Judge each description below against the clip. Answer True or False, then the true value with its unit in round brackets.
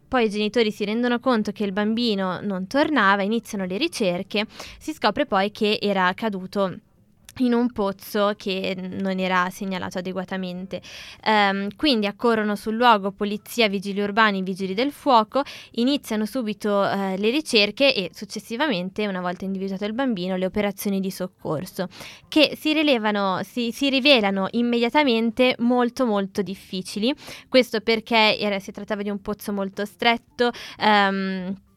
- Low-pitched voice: False (210 Hz)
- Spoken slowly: False (145 wpm)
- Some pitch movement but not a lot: True (3.4 semitones)